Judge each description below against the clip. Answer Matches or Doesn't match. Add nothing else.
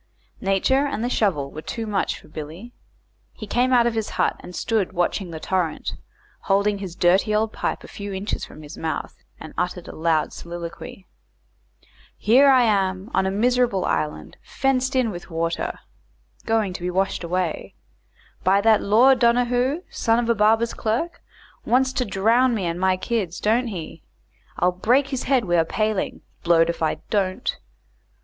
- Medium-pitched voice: Doesn't match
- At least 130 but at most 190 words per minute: Matches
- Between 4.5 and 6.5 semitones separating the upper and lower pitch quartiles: Matches